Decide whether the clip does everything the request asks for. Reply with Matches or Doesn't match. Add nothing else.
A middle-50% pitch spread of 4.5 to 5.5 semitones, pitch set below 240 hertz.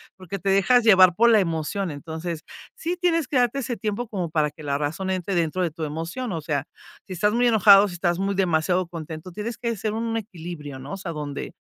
Matches